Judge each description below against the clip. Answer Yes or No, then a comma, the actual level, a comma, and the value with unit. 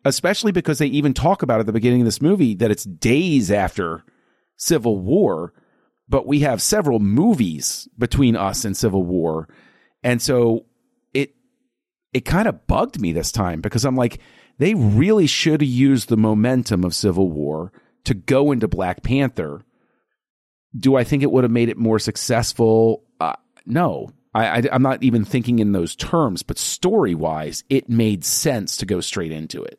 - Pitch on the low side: Yes, low, 120 Hz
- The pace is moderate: Yes, average, 175 wpm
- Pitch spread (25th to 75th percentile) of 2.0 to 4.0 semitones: No, average, 4.5 semitones